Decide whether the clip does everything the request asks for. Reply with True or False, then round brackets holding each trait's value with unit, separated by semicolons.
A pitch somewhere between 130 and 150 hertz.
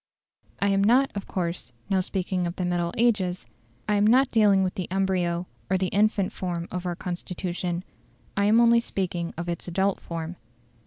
False (185 Hz)